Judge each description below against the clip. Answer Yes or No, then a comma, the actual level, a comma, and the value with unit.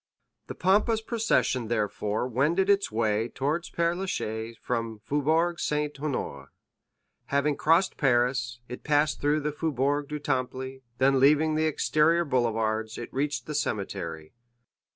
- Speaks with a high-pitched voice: No, medium, 140 Hz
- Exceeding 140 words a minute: No, slow, 135 wpm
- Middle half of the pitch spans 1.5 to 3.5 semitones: No, average, 4.7 semitones